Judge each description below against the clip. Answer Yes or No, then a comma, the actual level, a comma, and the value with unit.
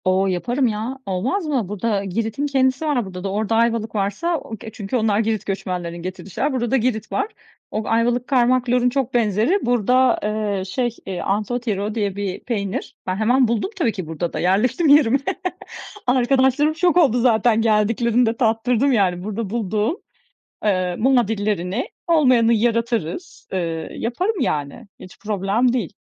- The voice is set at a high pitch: Yes, high, 225 Hz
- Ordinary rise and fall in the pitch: Yes, average, 4.0 semitones